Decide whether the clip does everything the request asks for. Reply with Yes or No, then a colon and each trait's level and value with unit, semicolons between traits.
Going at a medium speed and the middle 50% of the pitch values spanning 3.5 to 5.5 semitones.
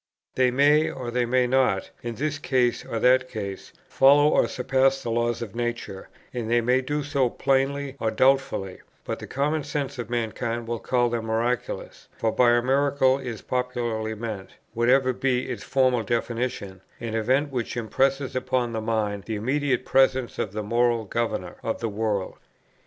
No: average, 170 wpm; average, 2.8 semitones